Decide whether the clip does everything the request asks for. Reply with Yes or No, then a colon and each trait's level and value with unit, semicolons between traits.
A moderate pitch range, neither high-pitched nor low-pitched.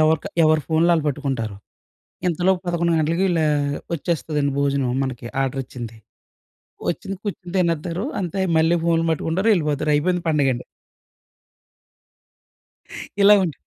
Yes: average, 3.4 semitones; medium, 160 Hz